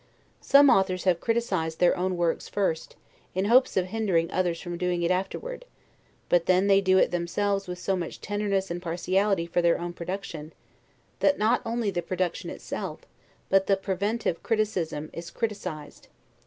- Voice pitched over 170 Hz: Yes, medium, 185 Hz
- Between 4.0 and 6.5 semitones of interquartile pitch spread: No, average, 2.8 semitones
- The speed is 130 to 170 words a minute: Yes, average, 165 wpm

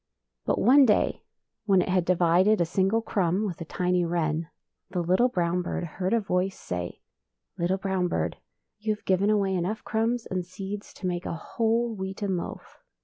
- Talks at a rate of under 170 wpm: No, average, 185 wpm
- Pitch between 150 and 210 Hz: Yes, medium, 185 Hz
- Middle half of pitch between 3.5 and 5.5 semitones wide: No, average, 3.0 semitones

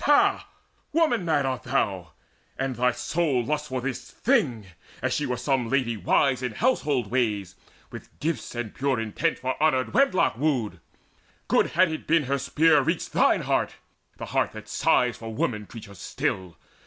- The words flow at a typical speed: Yes, average, 170 wpm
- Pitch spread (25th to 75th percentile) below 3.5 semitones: No, average, 5.1 semitones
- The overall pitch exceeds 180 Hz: No, low, 130 Hz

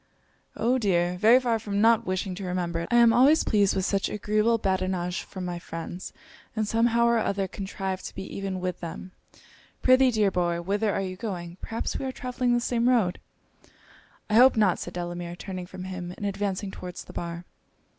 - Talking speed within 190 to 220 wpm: Yes, average, 195 wpm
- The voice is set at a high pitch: Yes, high, 195 Hz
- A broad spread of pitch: No, average, 4.1 semitones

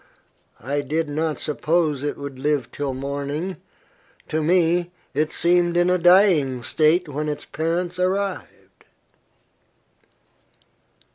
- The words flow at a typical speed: No, slow, 115 wpm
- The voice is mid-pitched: Yes, medium, 155 Hz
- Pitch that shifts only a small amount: No, average, 3.5 semitones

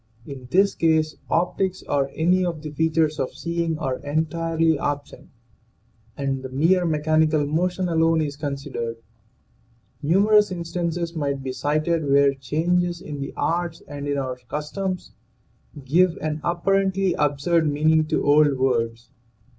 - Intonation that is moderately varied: Yes, average, 3.1 semitones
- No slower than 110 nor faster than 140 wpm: Yes, slow, 135 wpm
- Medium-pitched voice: Yes, medium, 155 Hz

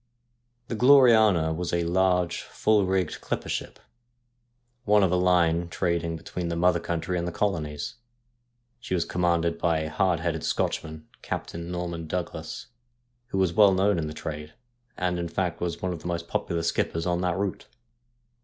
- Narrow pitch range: Yes, narrow, 1.9 semitones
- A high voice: No, very low, 85 Hz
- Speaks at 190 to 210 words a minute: No, average, 170 wpm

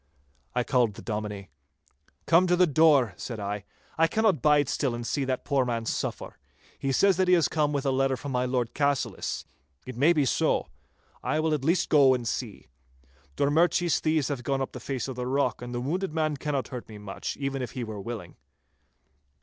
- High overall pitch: No, low, 135 Hz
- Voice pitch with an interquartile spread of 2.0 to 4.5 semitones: Yes, average, 3.9 semitones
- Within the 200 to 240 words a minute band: Yes, fast, 205 wpm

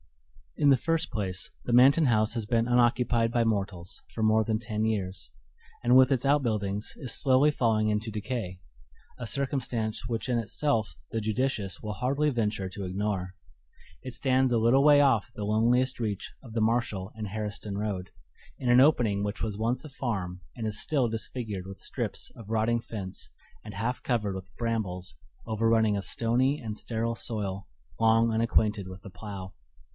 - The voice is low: Yes, low, 110 Hz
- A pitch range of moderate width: Yes, average, 3.0 semitones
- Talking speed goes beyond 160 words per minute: Yes, average, 170 wpm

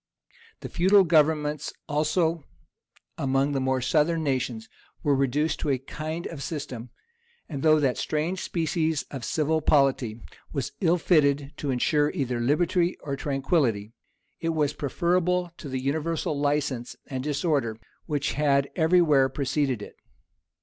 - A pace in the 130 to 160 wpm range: Yes, average, 140 wpm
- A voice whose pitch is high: No, medium, 150 Hz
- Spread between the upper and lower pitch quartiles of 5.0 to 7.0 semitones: No, average, 3.0 semitones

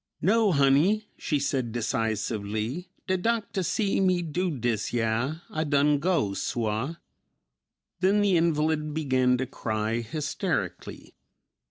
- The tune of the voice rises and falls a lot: Yes, wide, 7.1 semitones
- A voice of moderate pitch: Yes, medium, 145 Hz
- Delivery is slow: Yes, slow, 120 wpm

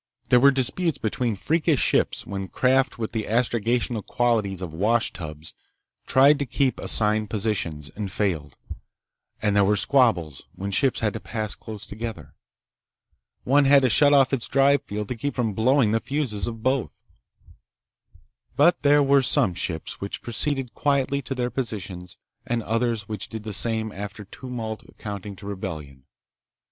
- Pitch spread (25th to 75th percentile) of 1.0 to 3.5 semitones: No, average, 4.6 semitones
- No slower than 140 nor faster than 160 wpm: Yes, average, 155 wpm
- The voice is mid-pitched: No, low, 115 Hz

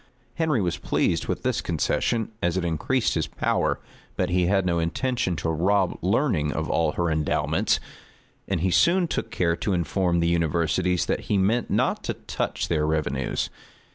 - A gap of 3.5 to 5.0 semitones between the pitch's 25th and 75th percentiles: No, average, 3.0 semitones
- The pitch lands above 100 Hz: No, very low, 85 Hz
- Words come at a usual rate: Yes, average, 170 wpm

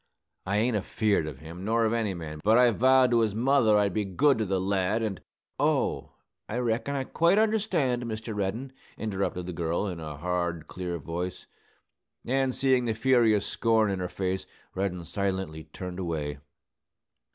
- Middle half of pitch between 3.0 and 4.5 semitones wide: No, average, 4.9 semitones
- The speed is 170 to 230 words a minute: Yes, average, 175 wpm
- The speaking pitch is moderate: No, low, 105 Hz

